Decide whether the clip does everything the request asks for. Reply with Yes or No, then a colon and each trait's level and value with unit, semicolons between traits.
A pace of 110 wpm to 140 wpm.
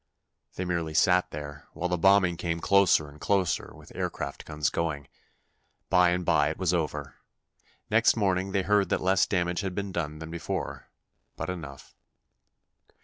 No: average, 160 wpm